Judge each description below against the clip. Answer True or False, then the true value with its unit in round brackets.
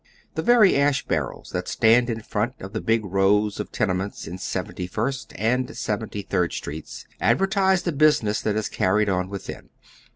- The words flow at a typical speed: True (170 wpm)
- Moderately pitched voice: False (110 Hz)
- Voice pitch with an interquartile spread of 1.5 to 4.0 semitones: False (4.8 semitones)